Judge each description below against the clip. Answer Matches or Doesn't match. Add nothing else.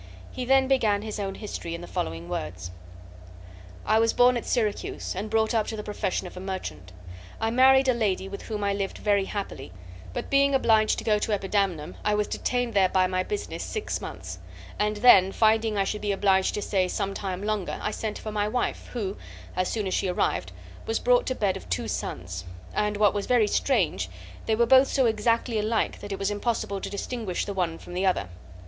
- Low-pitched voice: Doesn't match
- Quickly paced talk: Matches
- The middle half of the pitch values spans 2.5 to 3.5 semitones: Matches